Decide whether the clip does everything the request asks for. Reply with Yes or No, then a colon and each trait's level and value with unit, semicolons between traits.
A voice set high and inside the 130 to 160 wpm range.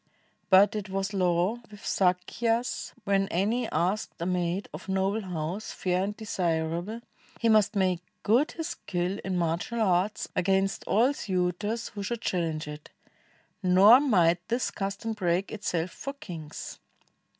Yes: high, 195 Hz; average, 140 wpm